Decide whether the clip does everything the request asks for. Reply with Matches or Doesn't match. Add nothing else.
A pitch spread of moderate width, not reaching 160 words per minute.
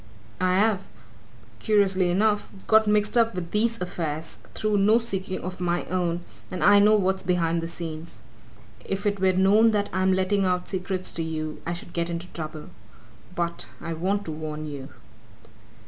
Doesn't match